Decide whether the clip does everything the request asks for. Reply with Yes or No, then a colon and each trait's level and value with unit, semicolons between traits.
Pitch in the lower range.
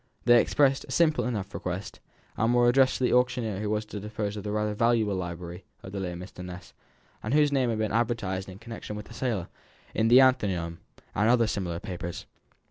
Yes: low, 105 Hz